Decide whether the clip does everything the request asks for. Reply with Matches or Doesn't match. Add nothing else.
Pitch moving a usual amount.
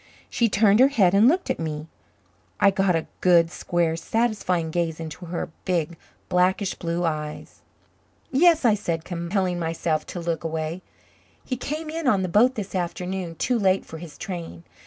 Matches